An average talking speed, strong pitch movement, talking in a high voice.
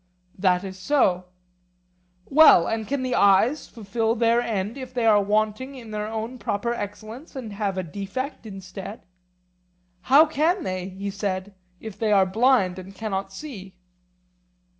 No: average, 150 wpm; average, 4.0 semitones; high, 215 Hz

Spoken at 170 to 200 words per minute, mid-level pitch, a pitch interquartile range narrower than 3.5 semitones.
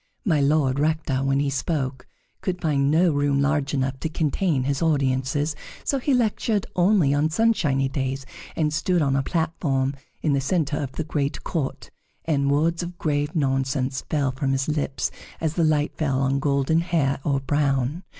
Yes: average, 175 wpm; medium, 145 Hz; average, 2.9 semitones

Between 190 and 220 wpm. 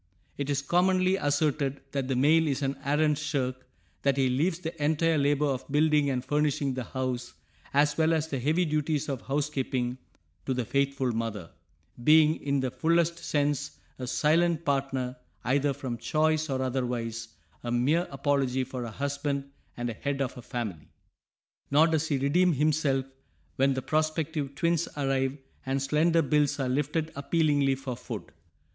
No: average, 160 wpm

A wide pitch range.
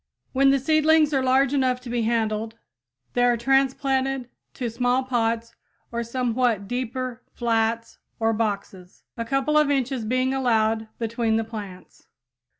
No: average, 2.8 semitones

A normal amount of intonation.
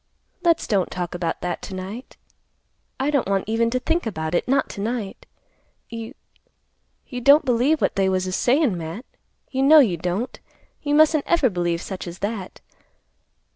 No: wide, 6.7 semitones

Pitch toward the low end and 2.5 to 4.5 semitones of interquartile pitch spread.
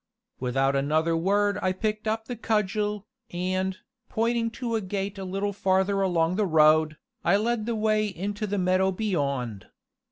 No: high, 195 Hz; average, 3.8 semitones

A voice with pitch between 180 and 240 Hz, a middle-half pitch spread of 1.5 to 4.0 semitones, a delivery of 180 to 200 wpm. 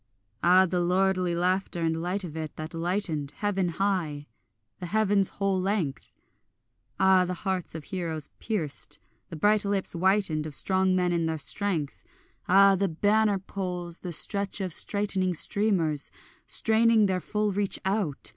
No: medium, 185 Hz; average, 3.0 semitones; average, 150 wpm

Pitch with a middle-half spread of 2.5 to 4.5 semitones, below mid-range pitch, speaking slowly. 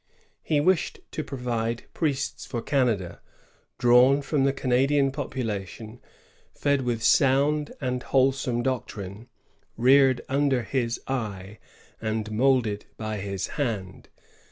Yes: average, 3.6 semitones; low, 125 Hz; slow, 110 wpm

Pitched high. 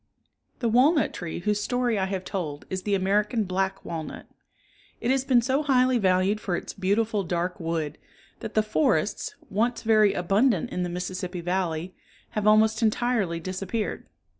Yes: high, 200 Hz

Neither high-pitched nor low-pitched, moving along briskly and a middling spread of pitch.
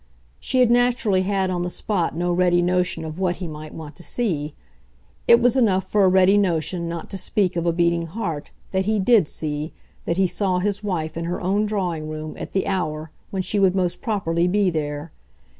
Yes: medium, 180 Hz; fast, 210 wpm; average, 3.1 semitones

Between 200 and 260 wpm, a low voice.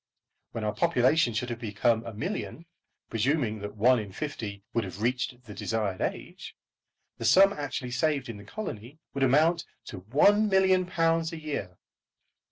No: average, 160 wpm; low, 125 Hz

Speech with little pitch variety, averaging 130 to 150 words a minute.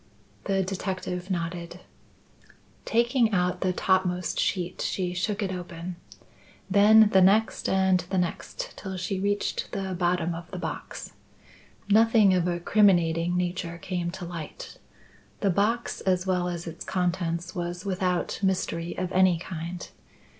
Yes: narrow, 1.8 semitones; average, 140 wpm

